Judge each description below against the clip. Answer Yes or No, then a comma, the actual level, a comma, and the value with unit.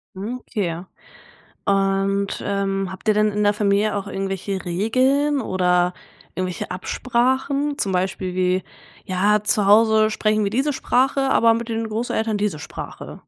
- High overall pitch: Yes, high, 205 Hz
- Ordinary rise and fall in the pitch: Yes, average, 3.0 semitones